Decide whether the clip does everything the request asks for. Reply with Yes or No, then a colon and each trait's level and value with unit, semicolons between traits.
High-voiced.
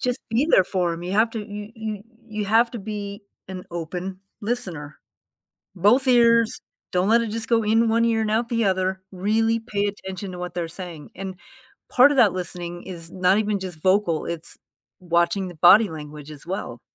Yes: high, 195 Hz